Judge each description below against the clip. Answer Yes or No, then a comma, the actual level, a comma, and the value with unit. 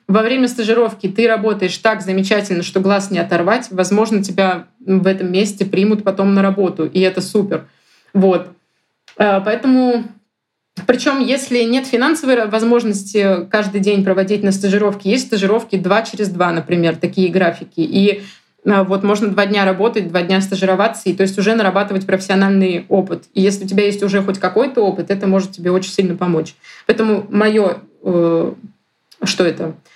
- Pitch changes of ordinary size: No, narrow, 2.3 semitones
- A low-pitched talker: No, high, 200 Hz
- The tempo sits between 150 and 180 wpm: Yes, fast, 160 wpm